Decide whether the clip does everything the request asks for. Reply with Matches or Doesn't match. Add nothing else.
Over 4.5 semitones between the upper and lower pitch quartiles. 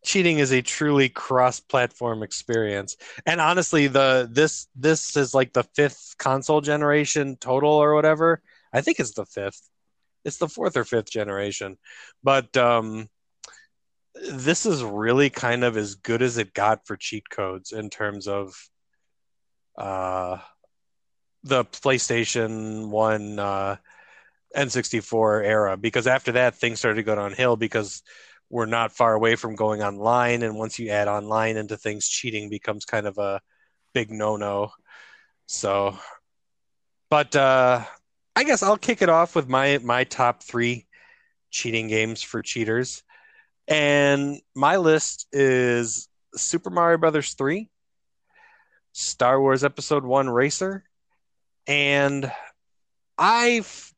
Matches